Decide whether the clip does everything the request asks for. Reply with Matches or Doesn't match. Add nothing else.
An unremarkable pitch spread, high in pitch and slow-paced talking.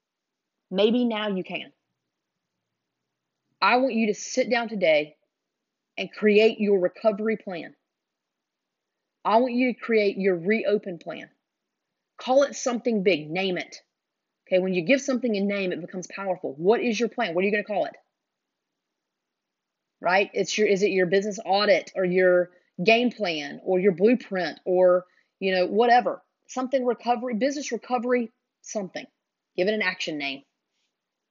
Doesn't match